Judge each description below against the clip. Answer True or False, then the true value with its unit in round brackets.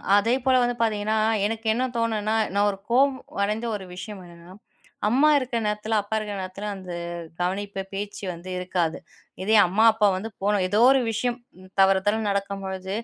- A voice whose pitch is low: False (210 Hz)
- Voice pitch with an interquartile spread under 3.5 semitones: True (2.6 semitones)